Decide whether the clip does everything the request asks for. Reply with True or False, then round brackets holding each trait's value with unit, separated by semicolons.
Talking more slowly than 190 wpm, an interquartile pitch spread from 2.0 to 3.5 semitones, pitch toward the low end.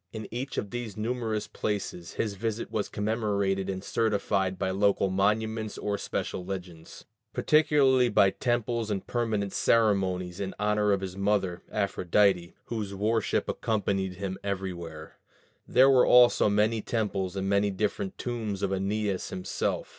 True (140 wpm; 2.5 semitones; 100 Hz)